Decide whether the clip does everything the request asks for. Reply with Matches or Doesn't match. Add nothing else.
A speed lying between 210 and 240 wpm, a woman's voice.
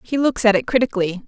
Matches